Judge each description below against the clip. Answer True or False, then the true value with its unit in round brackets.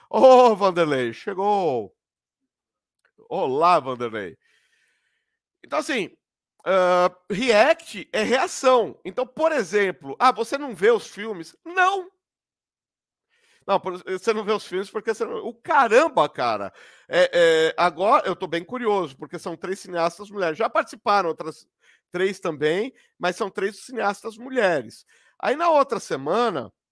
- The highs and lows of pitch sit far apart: True (6.3 semitones)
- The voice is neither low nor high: False (205 Hz)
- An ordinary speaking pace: True (135 wpm)